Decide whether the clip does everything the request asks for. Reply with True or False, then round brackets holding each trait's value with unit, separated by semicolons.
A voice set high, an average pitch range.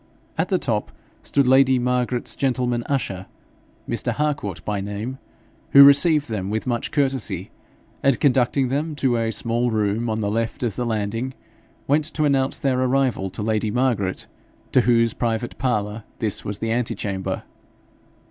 False (120 Hz; 3.5 semitones)